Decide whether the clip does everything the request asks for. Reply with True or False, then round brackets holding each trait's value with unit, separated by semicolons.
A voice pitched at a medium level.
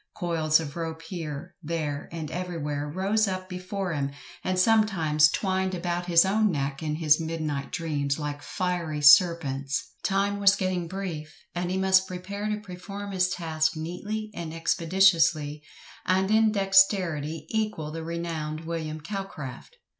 True (170 Hz)